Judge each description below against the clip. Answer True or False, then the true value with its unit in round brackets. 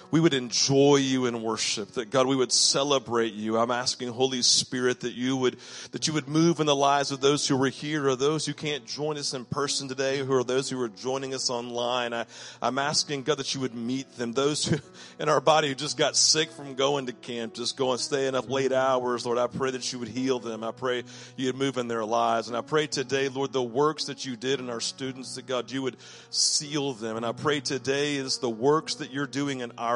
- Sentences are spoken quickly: True (250 wpm)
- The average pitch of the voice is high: False (130 Hz)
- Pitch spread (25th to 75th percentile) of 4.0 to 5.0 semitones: False (2.5 semitones)